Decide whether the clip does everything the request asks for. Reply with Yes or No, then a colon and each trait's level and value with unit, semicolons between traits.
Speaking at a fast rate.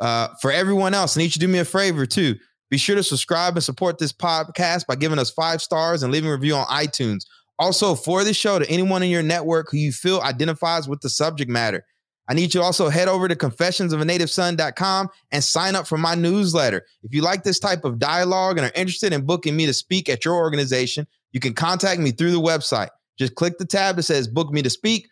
Yes: fast, 235 wpm